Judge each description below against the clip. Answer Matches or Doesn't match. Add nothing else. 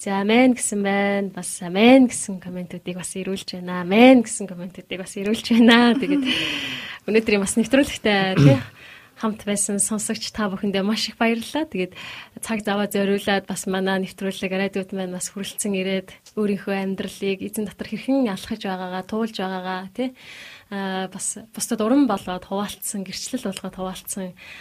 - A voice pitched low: Doesn't match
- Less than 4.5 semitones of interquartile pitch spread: Matches